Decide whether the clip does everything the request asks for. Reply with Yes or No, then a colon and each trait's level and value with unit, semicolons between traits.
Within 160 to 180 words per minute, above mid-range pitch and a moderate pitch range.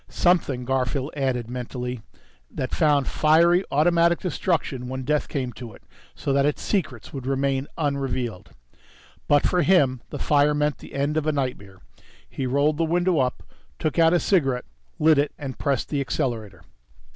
No: average, 165 wpm; medium, 140 Hz; average, 3.4 semitones